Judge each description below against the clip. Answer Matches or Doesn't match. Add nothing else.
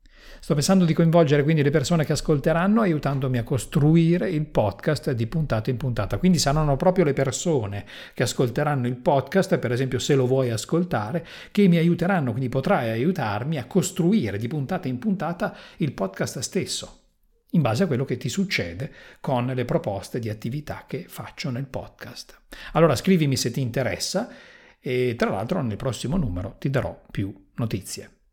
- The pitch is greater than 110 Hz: Matches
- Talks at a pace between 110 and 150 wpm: Doesn't match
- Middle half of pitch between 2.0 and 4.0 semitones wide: Doesn't match